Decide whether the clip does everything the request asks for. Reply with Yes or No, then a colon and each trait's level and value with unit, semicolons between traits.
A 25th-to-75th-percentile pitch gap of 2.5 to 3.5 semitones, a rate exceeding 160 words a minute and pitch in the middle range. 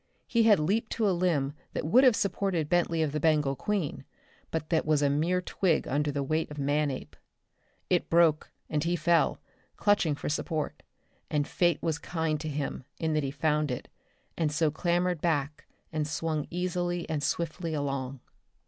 Yes: average, 2.9 semitones; average, 175 wpm; medium, 155 Hz